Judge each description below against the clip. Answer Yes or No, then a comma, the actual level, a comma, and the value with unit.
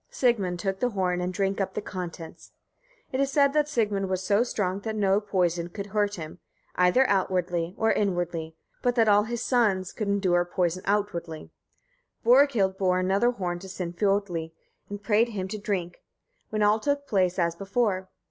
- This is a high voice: Yes, high, 195 Hz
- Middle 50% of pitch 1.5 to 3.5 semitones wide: Yes, average, 3.0 semitones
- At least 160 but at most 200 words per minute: Yes, average, 175 wpm